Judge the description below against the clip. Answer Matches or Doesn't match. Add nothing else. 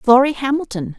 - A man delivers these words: Doesn't match